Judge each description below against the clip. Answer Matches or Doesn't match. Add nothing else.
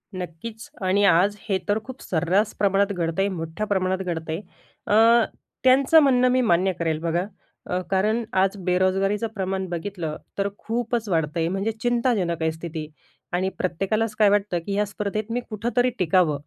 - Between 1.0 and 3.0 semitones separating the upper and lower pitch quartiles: Doesn't match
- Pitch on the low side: Doesn't match